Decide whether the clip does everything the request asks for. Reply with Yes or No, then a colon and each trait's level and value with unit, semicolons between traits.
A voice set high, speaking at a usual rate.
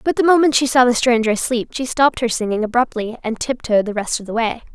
No: high, 240 Hz; fast, 255 wpm